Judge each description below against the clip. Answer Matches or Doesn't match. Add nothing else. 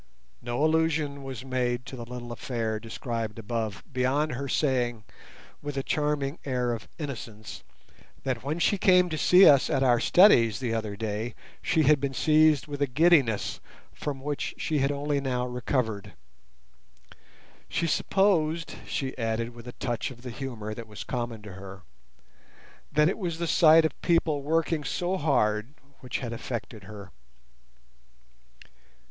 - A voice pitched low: Matches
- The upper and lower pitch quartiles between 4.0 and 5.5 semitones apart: Matches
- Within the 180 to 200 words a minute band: Doesn't match